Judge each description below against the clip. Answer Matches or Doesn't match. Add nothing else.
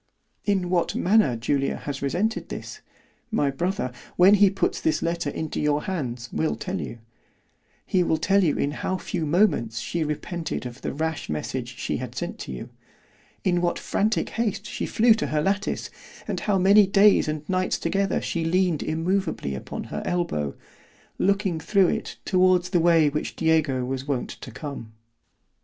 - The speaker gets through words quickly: Doesn't match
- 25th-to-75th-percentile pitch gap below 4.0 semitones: Doesn't match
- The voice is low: Doesn't match